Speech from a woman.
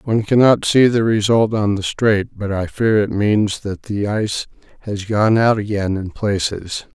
No: male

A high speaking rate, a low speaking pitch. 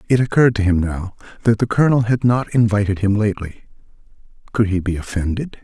No: average, 170 wpm; low, 105 Hz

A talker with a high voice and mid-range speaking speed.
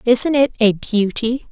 Yes: high, 235 Hz; average, 160 wpm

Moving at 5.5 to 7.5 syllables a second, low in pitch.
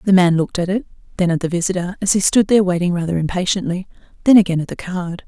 No: 7.0 syllables/s; medium, 185 Hz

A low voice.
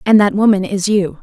No: high, 200 Hz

